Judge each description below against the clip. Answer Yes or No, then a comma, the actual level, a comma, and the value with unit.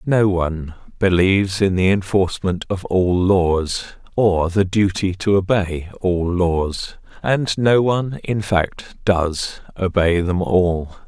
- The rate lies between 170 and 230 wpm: No, slow, 135 wpm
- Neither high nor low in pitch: No, very low, 95 Hz